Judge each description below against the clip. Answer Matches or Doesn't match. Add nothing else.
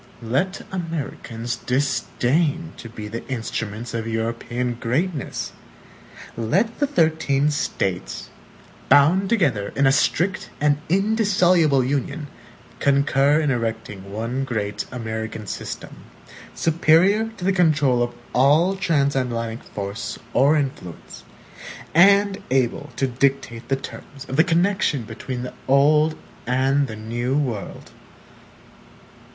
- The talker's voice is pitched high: Doesn't match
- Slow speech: Matches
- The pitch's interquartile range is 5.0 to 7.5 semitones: Matches